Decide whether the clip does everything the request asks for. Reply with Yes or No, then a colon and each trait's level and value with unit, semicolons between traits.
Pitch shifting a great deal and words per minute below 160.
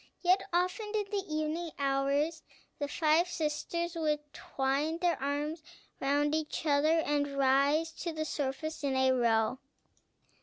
No: average, 2.8 semitones; average, 140 wpm